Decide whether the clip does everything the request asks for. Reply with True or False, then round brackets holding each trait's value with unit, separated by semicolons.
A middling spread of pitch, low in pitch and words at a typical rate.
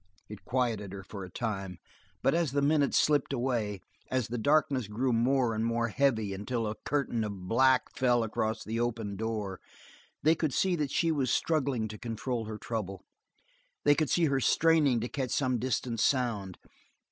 True (4.0 semitones; 120 Hz; 180 wpm)